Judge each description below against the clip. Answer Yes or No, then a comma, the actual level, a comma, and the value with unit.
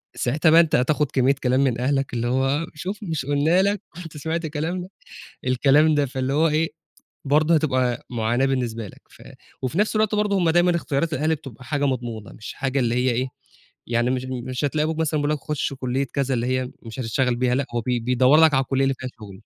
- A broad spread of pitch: No, average, 3.7 semitones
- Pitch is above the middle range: No, low, 135 Hz